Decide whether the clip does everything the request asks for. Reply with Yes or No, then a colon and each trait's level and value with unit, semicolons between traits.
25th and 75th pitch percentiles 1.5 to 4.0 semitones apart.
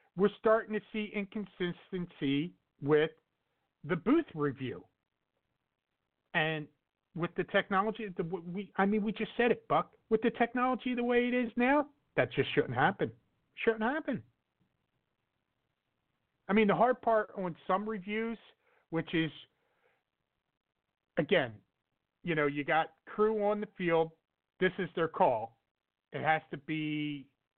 No: wide, 5.5 semitones